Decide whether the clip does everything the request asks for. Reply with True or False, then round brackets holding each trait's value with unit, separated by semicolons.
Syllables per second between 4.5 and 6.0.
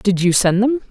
True (5.0 syllables/s)